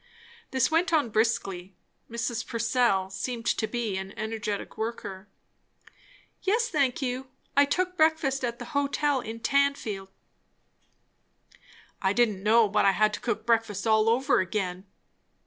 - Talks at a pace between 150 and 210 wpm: No, slow, 135 wpm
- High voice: Yes, high, 230 Hz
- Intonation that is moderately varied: Yes, average, 4.4 semitones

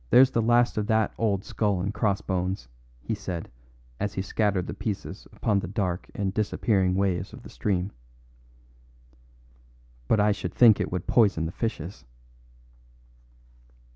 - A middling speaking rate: Yes, average, 145 wpm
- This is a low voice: Yes, low, 100 Hz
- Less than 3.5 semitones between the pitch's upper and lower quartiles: Yes, average, 2.7 semitones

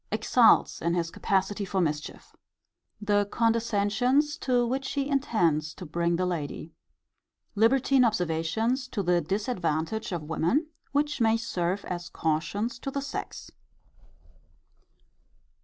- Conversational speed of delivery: No, slow, 120 wpm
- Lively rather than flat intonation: Yes, wide, 6.3 semitones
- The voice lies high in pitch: Yes, high, 205 Hz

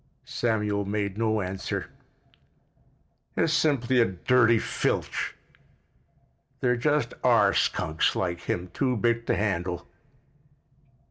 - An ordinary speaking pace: No, slow, 105 wpm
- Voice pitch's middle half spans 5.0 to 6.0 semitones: No, average, 4.4 semitones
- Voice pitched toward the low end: Yes, low, 110 Hz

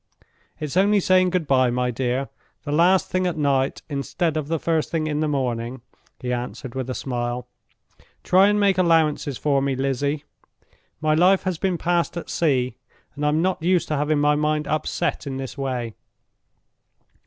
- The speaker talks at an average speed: Yes, average, 175 wpm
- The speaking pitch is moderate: Yes, medium, 150 Hz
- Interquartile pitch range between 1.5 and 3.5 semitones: No, average, 4.3 semitones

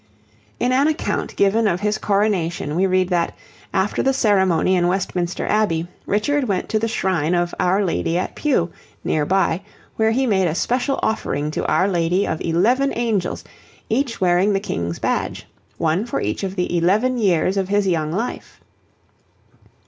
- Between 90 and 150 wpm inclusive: No, average, 170 wpm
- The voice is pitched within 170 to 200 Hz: Yes, high, 190 Hz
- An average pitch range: Yes, average, 4.0 semitones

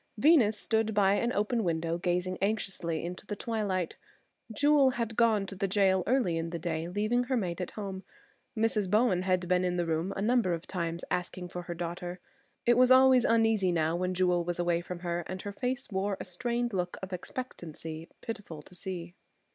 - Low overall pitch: No, high, 190 Hz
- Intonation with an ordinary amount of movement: Yes, average, 4.2 semitones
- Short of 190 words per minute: No, average, 195 wpm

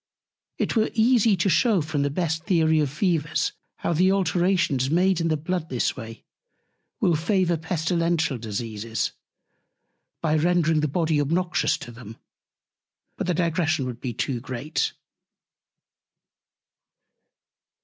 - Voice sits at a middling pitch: Yes, medium, 160 Hz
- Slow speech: Yes, slow, 130 wpm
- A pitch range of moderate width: Yes, average, 4.0 semitones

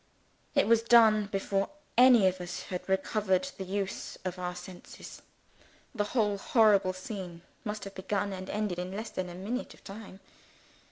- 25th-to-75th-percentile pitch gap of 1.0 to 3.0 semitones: Yes, narrow, 2.5 semitones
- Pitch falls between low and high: No, high, 195 Hz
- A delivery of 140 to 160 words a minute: No, average, 170 wpm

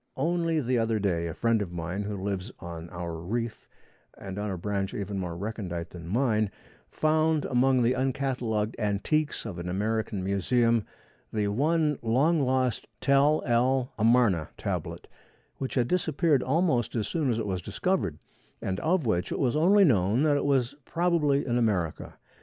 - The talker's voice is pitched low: Yes, low, 115 Hz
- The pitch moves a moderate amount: No, wide, 5.9 semitones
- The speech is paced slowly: No, average, 165 wpm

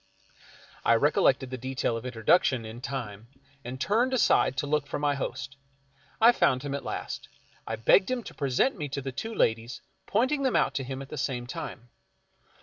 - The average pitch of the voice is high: No, low, 135 Hz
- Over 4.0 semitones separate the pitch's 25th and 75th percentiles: No, average, 3.6 semitones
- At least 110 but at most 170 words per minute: No, average, 190 wpm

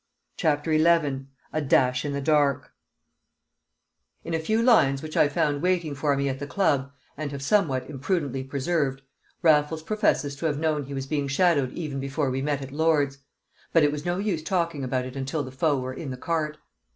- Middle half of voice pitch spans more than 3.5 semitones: No, average, 2.8 semitones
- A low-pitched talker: No, medium, 145 Hz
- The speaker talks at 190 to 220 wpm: Yes, average, 195 wpm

